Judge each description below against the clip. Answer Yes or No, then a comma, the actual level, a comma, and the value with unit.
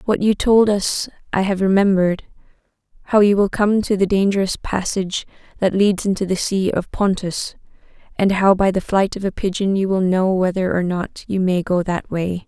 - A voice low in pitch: No, high, 190 Hz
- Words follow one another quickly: No, average, 190 wpm